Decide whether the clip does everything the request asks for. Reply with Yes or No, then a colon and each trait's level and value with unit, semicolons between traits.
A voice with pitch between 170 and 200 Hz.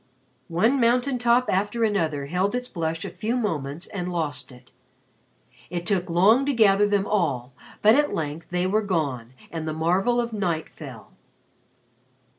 Yes: medium, 185 Hz